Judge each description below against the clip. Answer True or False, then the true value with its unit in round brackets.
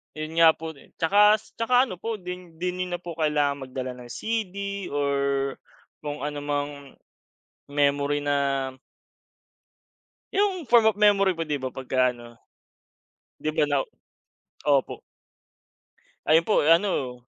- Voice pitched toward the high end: False (160 Hz)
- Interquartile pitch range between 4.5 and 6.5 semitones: True (5.6 semitones)